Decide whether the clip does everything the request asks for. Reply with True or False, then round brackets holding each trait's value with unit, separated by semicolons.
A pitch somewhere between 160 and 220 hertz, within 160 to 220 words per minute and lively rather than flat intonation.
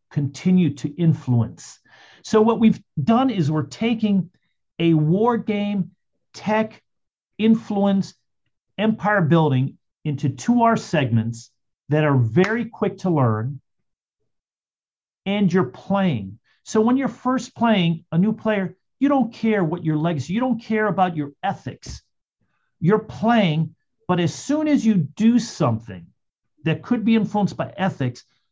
False (185 Hz; 135 wpm; 6.4 semitones)